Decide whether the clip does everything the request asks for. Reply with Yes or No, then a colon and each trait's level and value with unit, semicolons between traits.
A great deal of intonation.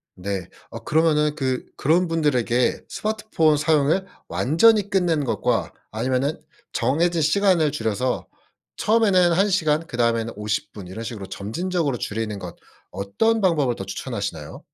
Yes: wide, 7.2 semitones